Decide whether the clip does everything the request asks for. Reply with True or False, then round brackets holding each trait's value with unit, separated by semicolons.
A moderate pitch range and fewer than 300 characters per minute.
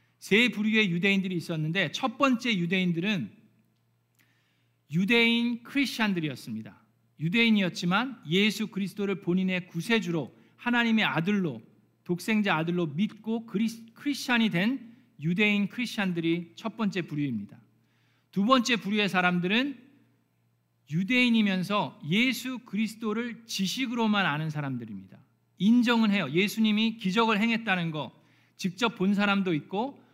False (4.8 semitones; 305 characters per minute)